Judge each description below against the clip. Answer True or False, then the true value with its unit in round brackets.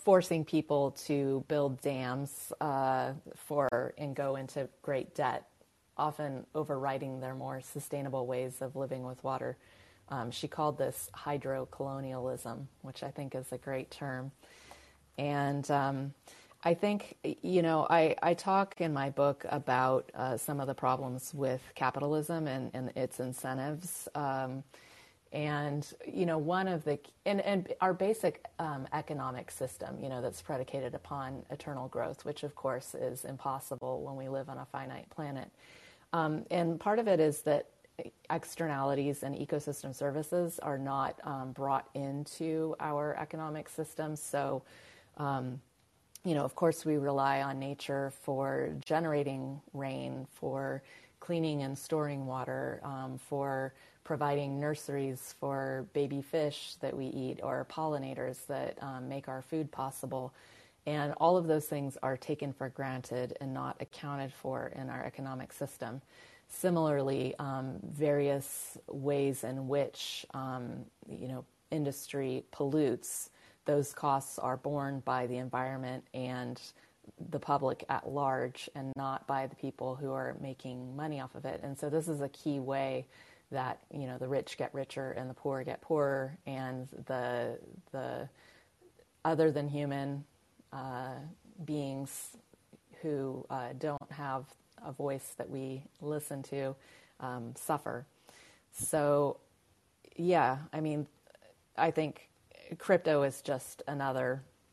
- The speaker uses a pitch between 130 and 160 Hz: True (140 Hz)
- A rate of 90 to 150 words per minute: True (140 wpm)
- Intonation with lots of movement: False (2.1 semitones)